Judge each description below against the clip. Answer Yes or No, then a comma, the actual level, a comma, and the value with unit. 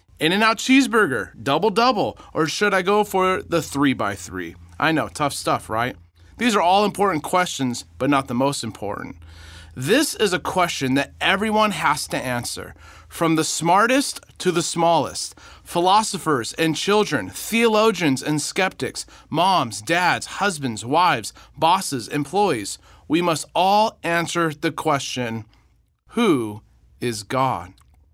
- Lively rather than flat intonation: Yes, wide, 8.1 semitones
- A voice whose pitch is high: No, medium, 155 Hz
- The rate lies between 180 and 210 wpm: No, average, 140 wpm